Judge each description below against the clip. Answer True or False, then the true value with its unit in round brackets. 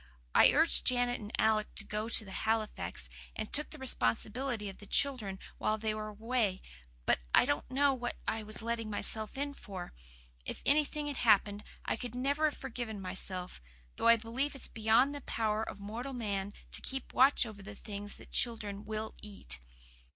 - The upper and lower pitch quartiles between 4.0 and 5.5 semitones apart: False (3.6 semitones)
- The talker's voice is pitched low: False (220 Hz)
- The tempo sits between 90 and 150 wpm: False (180 wpm)